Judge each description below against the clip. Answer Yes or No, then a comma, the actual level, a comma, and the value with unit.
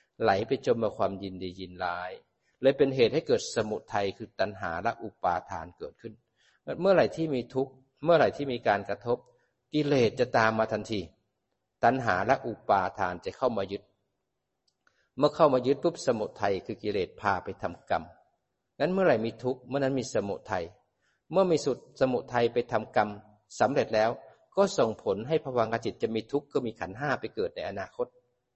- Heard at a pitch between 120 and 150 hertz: Yes, low, 125 Hz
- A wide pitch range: Yes, wide, 5.8 semitones